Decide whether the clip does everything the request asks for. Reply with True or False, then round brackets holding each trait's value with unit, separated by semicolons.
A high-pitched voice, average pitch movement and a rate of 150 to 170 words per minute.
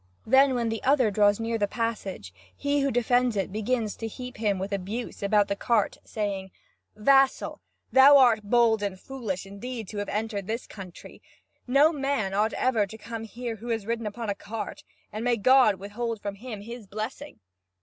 False (225 Hz; 3.2 semitones; 185 wpm)